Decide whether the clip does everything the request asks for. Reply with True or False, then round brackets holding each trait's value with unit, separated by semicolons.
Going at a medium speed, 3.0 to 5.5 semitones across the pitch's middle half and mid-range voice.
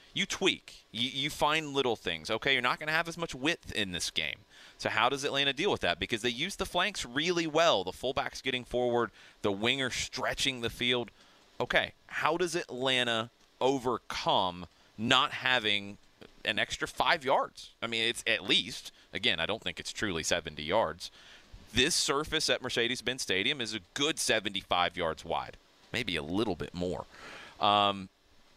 False (175 wpm; 4.6 semitones; 125 Hz)